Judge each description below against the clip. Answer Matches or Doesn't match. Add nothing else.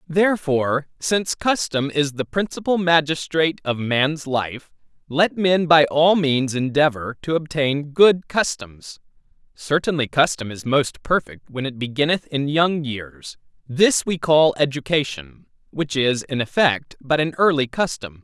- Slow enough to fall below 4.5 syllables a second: Matches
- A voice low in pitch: Doesn't match